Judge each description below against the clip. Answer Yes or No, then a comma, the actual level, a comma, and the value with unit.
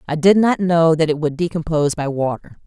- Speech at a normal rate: No, fast, 225 wpm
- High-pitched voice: No, medium, 160 Hz